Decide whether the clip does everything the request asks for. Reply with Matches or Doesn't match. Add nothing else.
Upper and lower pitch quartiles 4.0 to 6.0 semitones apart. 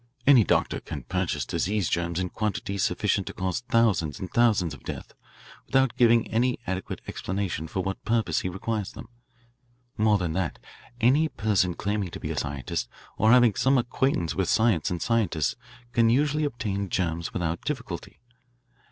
Matches